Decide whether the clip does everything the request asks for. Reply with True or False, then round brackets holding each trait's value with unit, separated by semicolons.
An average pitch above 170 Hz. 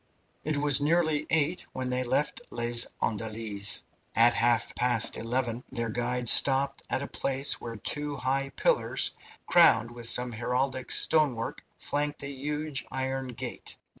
False (130 Hz)